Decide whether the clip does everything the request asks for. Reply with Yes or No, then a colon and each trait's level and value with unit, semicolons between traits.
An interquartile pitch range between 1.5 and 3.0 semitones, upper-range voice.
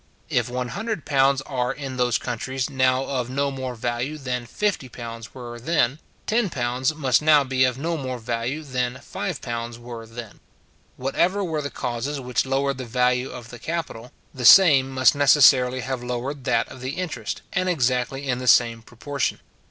No: narrow, 2.4 semitones; low, 130 Hz